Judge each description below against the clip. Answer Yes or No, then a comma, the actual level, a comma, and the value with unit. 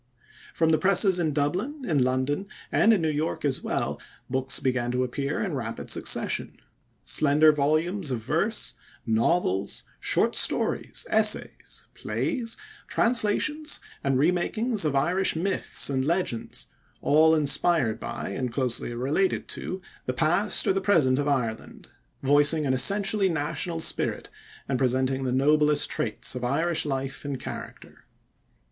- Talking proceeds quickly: No, average, 140 wpm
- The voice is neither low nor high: Yes, medium, 150 Hz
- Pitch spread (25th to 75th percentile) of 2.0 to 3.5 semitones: No, average, 5.3 semitones